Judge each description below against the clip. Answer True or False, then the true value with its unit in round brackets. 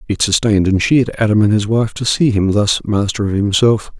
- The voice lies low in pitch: True (105 Hz)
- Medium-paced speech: False (225 wpm)